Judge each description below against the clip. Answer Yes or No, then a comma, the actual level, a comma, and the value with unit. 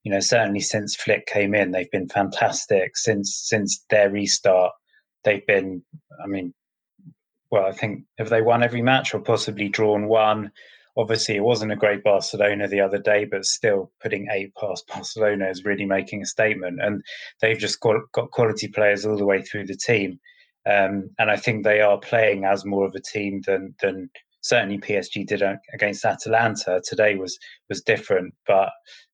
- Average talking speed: Yes, average, 180 wpm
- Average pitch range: No, narrow, 2.2 semitones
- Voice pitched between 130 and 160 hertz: No, low, 105 Hz